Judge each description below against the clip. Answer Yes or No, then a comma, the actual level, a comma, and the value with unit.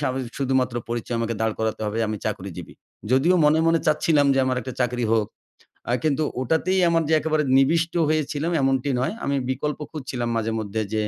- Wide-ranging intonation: No, average, 4.8 semitones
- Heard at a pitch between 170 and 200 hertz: No, low, 135 Hz